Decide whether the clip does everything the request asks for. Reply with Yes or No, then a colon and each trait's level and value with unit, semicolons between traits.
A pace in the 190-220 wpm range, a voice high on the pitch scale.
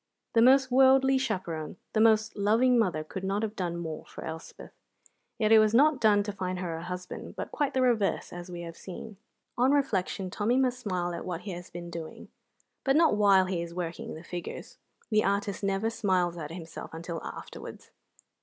Yes: average, 195 wpm; high, 195 Hz